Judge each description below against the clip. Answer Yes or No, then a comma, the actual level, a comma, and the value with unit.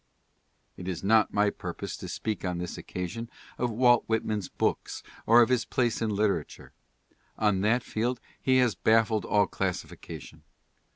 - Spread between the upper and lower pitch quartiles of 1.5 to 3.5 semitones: Yes, average, 3.2 semitones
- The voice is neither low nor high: No, low, 110 Hz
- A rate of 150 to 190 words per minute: Yes, average, 160 wpm